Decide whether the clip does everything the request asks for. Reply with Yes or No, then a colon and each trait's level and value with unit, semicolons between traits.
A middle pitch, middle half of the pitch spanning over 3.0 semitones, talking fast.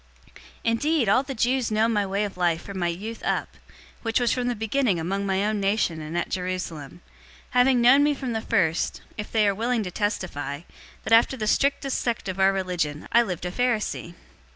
No: high, 210 Hz; average, 4.7 semitones; fast, 210 wpm